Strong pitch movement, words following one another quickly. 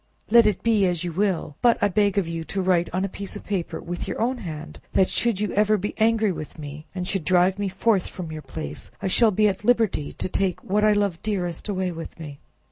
No: average, 3.4 semitones; fast, 245 wpm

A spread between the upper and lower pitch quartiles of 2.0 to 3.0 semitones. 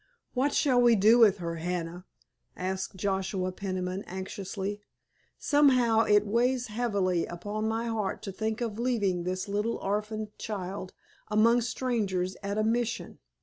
No: average, 3.6 semitones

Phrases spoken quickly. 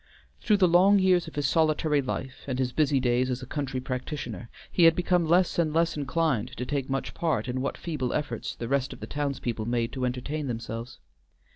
Yes: fast, 210 wpm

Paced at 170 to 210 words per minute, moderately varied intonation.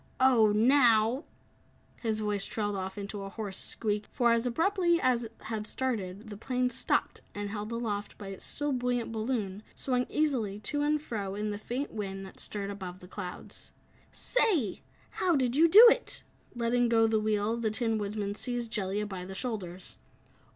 Yes: average, 180 wpm; average, 3.4 semitones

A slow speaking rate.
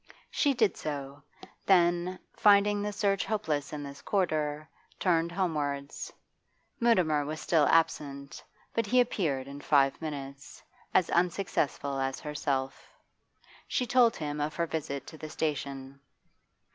Yes: slow, 130 wpm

